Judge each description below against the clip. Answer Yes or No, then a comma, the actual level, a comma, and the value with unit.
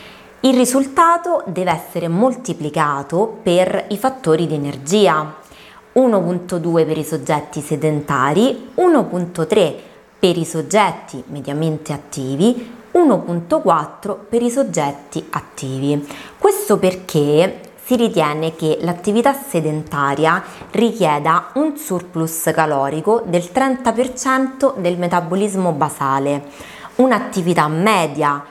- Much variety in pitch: Yes, wide, 6.9 semitones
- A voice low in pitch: No, medium, 175 Hz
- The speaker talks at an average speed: No, slow, 95 wpm